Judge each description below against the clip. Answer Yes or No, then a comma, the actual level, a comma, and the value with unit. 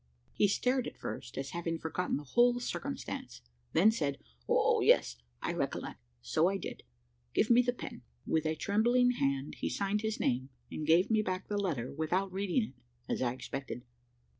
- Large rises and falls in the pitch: Yes, wide, 7.7 semitones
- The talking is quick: No, average, 180 wpm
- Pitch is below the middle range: No, medium, 180 Hz